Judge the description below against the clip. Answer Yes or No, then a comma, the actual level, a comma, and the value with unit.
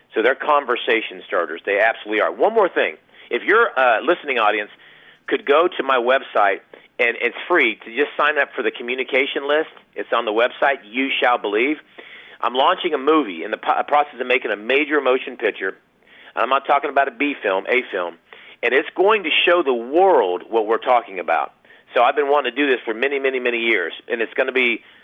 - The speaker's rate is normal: No, fast, 210 wpm